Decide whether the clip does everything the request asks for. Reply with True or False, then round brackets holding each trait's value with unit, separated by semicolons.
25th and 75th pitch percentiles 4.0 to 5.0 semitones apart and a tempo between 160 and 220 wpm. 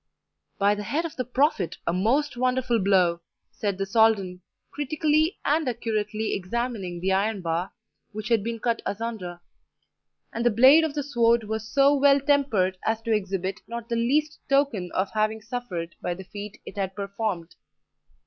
True (4.7 semitones; 170 wpm)